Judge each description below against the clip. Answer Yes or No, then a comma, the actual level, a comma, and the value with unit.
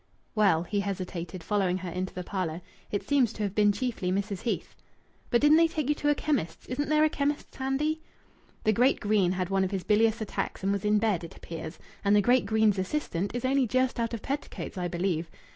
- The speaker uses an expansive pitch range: Yes, wide, 5.7 semitones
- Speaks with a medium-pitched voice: No, high, 210 Hz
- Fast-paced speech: Yes, fast, 220 wpm